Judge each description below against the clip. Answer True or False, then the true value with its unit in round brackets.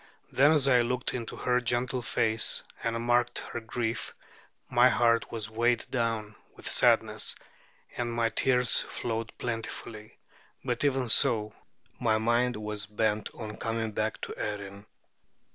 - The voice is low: True (115 Hz)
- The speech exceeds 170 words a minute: False (140 wpm)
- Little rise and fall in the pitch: True (2.0 semitones)